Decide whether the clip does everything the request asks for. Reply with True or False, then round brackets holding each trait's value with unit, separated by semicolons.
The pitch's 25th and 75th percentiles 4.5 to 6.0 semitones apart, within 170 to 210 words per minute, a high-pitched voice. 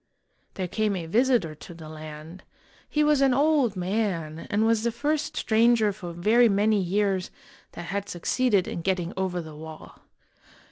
False (5.1 semitones; 160 wpm; 195 Hz)